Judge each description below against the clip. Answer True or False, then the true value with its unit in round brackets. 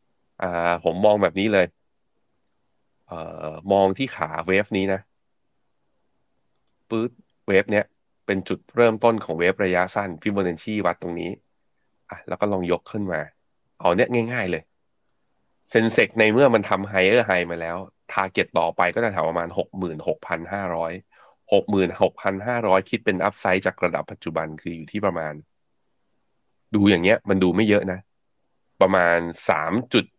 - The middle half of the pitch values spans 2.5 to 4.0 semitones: True (3.3 semitones)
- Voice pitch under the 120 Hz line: True (95 Hz)